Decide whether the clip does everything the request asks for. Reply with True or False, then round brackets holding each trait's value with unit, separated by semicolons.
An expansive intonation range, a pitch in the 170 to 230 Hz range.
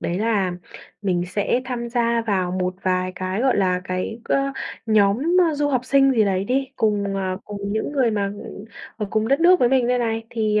False (4.3 semitones; 215 Hz)